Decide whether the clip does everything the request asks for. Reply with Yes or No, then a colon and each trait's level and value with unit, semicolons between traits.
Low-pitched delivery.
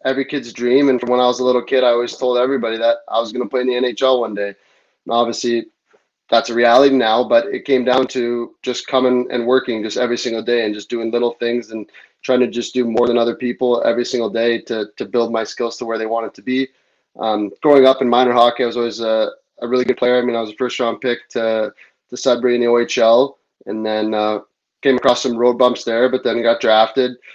Yes: low, 120 Hz